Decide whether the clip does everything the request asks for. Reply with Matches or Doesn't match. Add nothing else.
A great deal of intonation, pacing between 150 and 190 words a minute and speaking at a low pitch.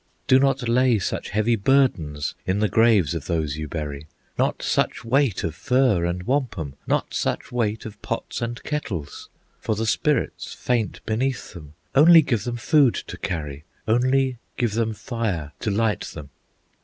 Matches